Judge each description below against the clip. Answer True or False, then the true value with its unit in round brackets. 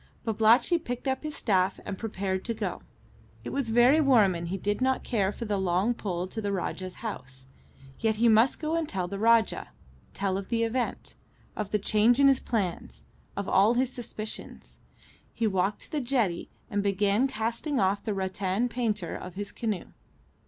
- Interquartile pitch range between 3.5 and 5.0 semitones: True (3.8 semitones)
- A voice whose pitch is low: False (215 Hz)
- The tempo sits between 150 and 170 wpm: False (185 wpm)